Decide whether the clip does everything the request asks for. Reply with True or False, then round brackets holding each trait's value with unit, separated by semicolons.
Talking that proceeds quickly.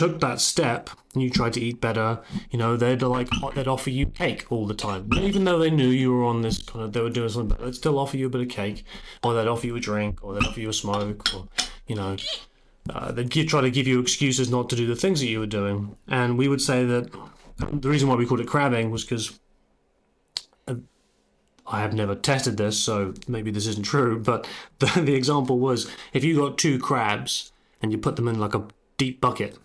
True (235 wpm)